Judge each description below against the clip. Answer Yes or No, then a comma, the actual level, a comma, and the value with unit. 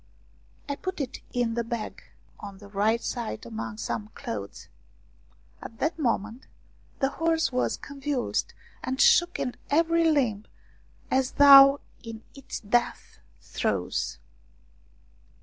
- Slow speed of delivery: Yes, slow, 120 wpm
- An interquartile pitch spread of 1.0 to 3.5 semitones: No, average, 5.2 semitones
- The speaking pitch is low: No, high, 245 Hz